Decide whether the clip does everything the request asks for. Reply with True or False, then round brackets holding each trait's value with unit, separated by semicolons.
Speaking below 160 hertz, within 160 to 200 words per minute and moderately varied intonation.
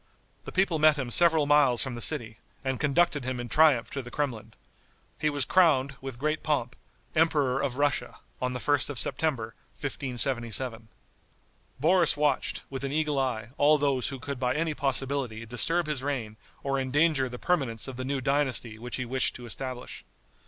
True (135 Hz; 180 wpm; 3.1 semitones)